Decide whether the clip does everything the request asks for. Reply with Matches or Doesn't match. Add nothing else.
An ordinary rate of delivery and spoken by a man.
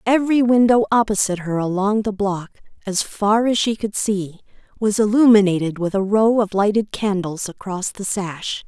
Doesn't match